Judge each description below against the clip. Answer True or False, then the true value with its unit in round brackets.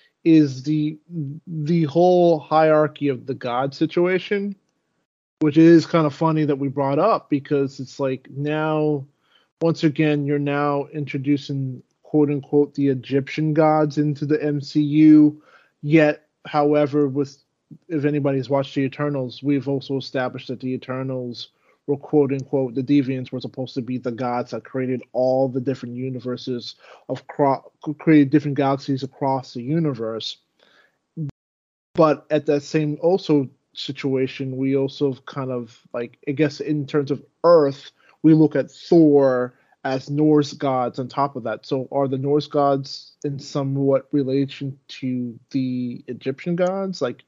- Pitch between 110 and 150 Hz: True (140 Hz)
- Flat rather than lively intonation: True (2.2 semitones)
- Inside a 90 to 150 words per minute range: True (145 wpm)